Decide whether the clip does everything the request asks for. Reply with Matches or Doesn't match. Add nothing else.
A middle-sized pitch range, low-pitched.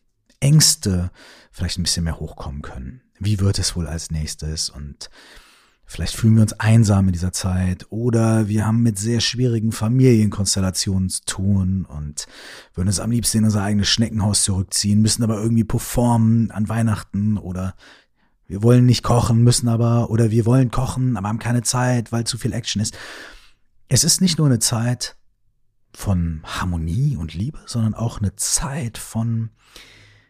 Matches